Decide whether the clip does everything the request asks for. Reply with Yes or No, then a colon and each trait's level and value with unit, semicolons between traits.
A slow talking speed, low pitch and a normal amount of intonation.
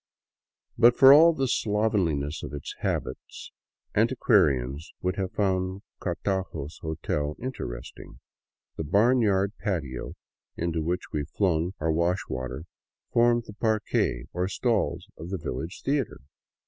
No: slow, 120 wpm; very low, 95 Hz; wide, 5.7 semitones